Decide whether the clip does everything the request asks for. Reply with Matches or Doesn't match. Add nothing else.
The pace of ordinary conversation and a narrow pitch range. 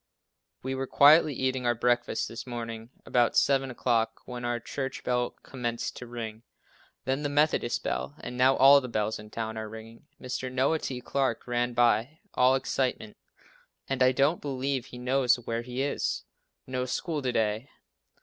Matches